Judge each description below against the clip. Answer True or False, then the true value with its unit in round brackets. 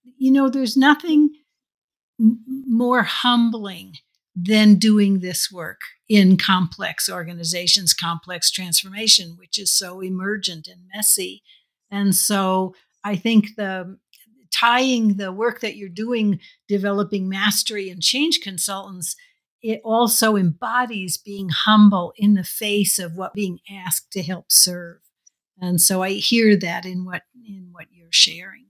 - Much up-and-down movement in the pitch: False (3.4 semitones)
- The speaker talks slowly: True (130 wpm)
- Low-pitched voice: False (200 Hz)